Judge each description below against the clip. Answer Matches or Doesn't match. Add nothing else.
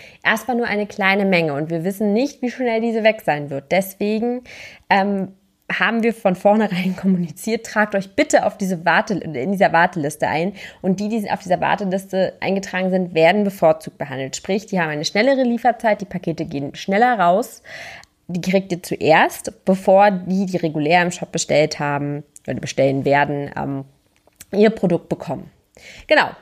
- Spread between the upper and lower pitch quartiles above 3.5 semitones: Matches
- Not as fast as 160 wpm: Doesn't match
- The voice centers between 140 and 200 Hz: Matches